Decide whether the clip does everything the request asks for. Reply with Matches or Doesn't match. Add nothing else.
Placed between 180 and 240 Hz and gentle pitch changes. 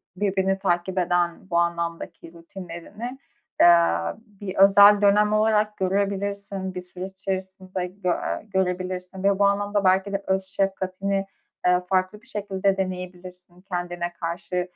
Matches